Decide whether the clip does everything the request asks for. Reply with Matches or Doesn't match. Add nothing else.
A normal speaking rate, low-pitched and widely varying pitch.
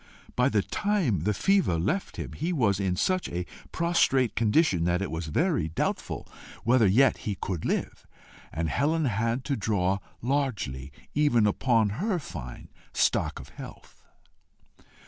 Matches